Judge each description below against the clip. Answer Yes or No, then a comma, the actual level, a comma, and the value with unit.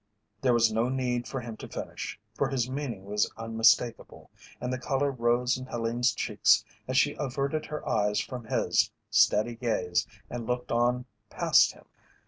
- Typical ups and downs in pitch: No, narrow, 2.2 semitones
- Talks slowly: No, average, 165 wpm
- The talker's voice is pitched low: Yes, low, 120 Hz